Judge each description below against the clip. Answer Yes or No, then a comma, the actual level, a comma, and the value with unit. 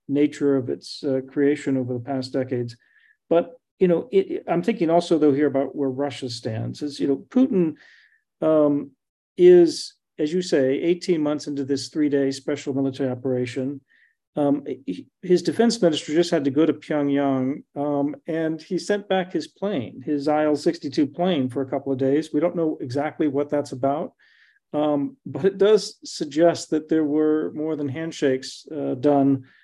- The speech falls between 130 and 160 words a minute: No, average, 170 wpm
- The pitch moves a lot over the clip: No, average, 3.8 semitones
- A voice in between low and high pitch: Yes, medium, 150 Hz